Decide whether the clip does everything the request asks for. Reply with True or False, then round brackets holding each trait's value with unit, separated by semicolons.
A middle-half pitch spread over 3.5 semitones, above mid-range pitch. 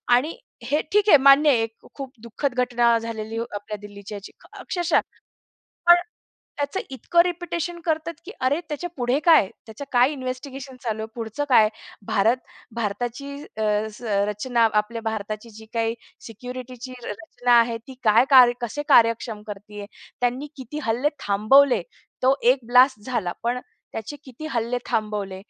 True (3.9 semitones; 245 Hz)